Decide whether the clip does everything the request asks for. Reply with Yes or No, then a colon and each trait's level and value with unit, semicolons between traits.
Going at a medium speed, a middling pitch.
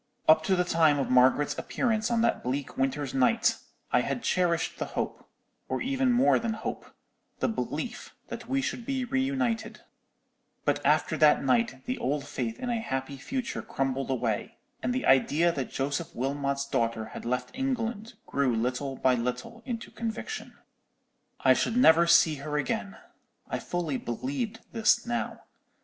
Yes: average, 155 wpm; medium, 160 Hz